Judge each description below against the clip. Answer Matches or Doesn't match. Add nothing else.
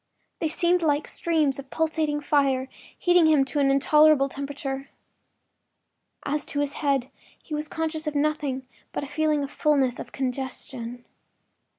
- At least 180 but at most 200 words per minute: Doesn't match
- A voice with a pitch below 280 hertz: Doesn't match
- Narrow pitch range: Matches